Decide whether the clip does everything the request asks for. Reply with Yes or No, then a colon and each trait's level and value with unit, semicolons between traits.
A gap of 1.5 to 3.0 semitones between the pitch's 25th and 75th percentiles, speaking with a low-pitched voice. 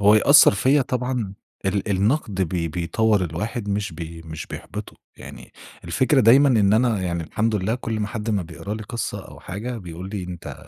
No: average, 4.3 semitones; low, 105 Hz